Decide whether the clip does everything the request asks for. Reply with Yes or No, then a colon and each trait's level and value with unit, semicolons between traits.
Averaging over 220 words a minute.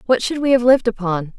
Yes: fast, 260 wpm